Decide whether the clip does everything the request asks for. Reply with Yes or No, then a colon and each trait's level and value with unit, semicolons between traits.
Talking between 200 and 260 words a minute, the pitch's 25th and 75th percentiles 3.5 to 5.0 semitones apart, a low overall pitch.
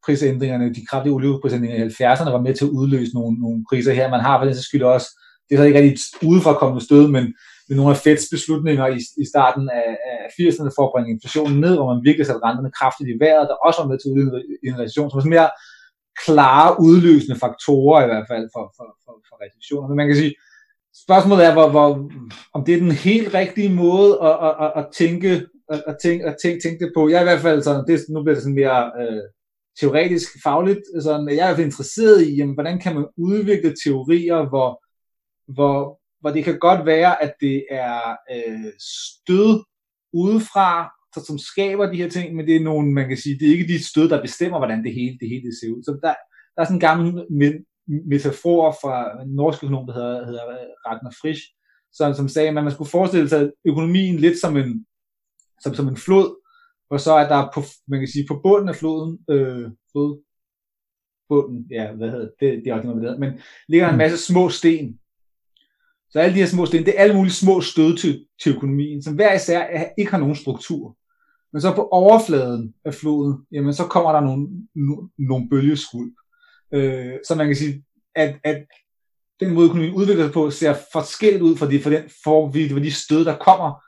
No: average, 210 wpm; average, 4.0 semitones; medium, 150 Hz